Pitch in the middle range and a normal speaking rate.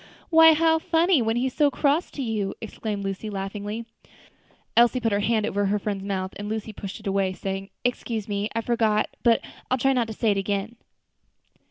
No: high, 220 Hz; average, 195 wpm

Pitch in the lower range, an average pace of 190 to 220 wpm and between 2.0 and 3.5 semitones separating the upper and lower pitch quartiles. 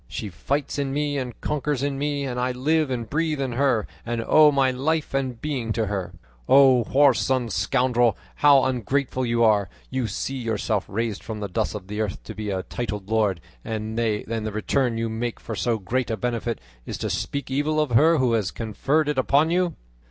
No: low, 125 Hz; average, 200 wpm; average, 4.1 semitones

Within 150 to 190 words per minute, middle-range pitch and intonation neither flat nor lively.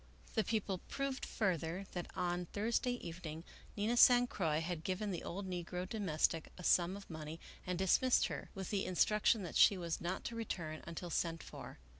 Yes: average, 180 wpm; medium, 180 Hz; average, 3.6 semitones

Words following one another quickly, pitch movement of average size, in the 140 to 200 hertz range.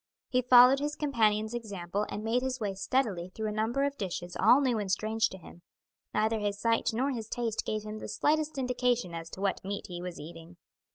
No: fast, 215 wpm; average, 4.3 semitones; high, 220 Hz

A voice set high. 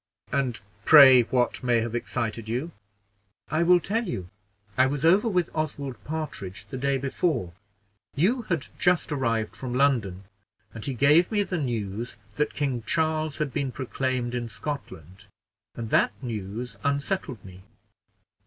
No: low, 130 Hz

